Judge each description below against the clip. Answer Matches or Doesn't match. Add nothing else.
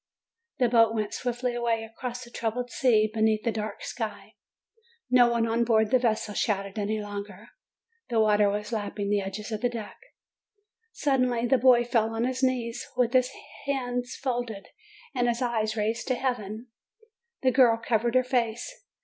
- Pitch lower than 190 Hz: Doesn't match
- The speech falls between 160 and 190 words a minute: Matches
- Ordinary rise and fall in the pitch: Doesn't match